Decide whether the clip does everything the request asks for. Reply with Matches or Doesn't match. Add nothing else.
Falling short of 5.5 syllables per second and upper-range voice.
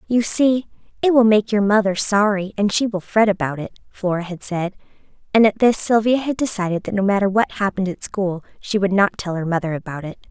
Doesn't match